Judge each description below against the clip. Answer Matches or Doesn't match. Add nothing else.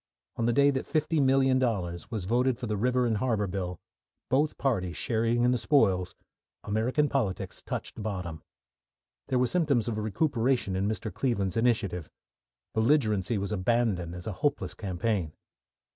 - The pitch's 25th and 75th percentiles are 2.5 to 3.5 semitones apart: Doesn't match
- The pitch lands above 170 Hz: Doesn't match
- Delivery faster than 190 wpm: Doesn't match